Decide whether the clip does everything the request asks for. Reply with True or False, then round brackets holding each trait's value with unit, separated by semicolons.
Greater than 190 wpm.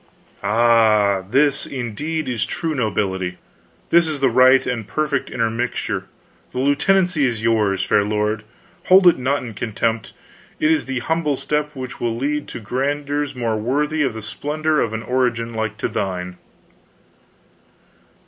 False (150 wpm)